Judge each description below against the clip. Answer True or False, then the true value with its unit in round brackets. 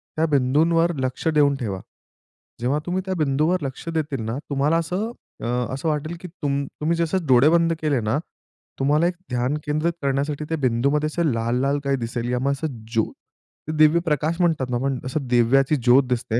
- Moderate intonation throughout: True (3.8 semitones)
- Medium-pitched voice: True (145 Hz)